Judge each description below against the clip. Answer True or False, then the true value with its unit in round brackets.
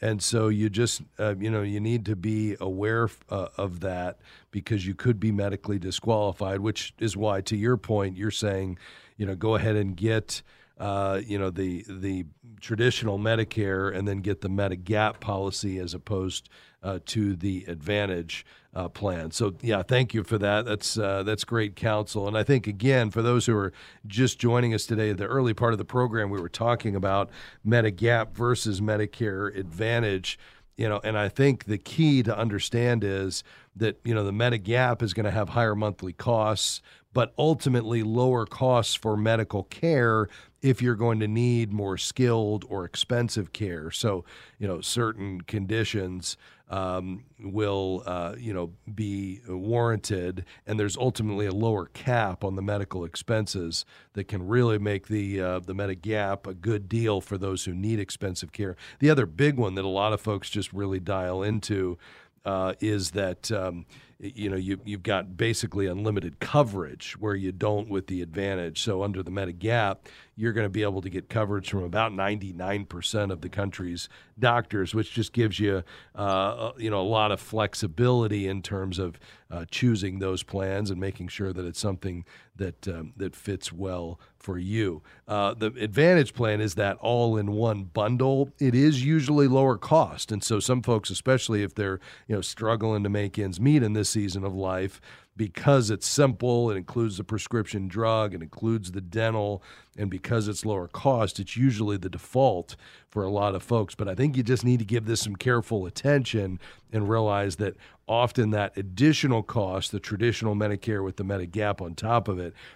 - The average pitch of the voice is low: True (105 Hz)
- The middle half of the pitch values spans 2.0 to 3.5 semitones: True (2.9 semitones)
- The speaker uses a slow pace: False (180 wpm)